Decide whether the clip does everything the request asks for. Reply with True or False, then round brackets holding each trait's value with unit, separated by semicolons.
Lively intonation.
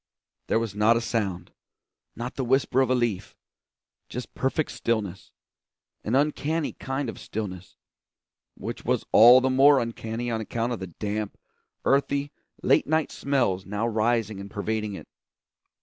False (3.9 semitones)